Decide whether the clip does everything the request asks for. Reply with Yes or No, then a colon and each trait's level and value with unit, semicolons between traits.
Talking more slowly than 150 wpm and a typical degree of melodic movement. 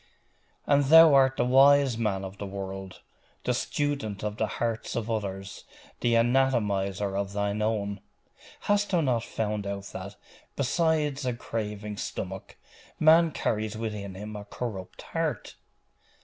Yes: average, 140 wpm; average, 4.8 semitones